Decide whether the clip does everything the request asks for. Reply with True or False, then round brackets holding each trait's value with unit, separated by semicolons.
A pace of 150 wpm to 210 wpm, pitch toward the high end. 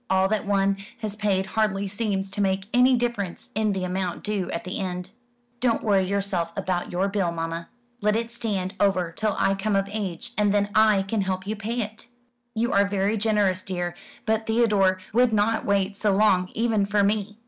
True (200 wpm; 200 Hz)